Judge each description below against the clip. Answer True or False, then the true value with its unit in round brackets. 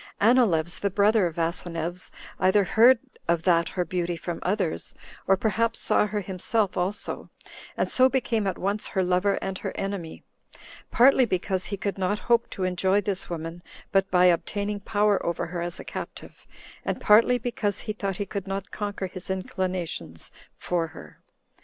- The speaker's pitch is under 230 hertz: True (190 Hz)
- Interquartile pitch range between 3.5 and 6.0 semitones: False (2.8 semitones)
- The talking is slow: False (170 wpm)